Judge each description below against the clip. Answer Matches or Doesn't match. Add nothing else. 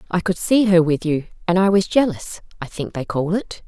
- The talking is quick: Matches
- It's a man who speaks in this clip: Doesn't match